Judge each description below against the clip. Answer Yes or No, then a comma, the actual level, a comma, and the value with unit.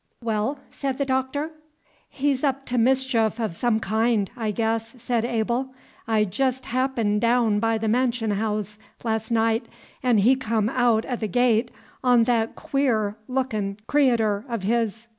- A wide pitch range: No, average, 2.7 semitones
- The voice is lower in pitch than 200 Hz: No, high, 230 Hz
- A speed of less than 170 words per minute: Yes, average, 155 wpm